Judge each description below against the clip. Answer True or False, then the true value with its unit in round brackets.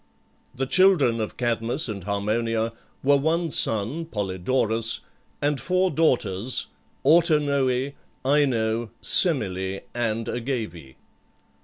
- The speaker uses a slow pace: True (95 wpm)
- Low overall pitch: True (120 Hz)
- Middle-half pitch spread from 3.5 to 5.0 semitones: True (4.7 semitones)